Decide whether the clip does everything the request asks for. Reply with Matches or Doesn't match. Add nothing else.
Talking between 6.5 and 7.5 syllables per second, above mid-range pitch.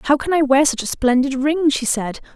Doesn't match